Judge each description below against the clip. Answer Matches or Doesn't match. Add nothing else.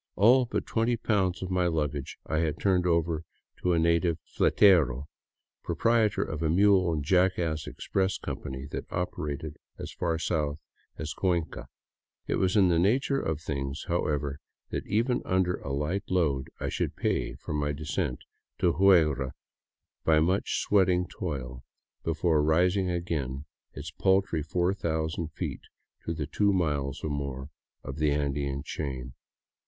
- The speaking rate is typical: Matches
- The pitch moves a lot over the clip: Doesn't match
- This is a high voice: Doesn't match